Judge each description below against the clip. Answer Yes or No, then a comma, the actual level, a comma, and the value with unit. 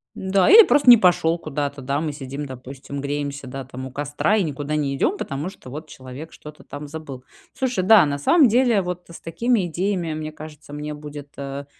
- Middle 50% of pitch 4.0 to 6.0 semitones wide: Yes, average, 4.3 semitones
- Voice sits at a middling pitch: Yes, medium, 150 Hz